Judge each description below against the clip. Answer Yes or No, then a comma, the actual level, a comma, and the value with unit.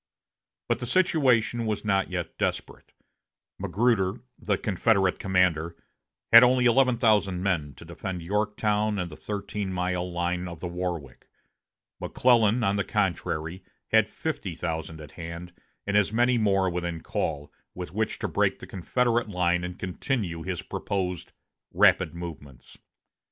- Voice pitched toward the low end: Yes, very low, 95 Hz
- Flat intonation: No, average, 3.8 semitones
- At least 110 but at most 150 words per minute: Yes, average, 140 wpm